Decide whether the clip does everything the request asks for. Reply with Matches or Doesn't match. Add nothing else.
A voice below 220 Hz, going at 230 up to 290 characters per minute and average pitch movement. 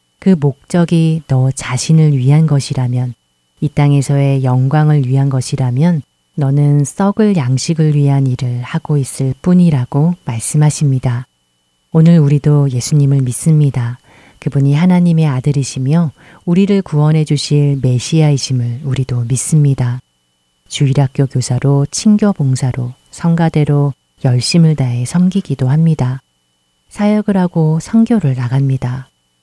Matches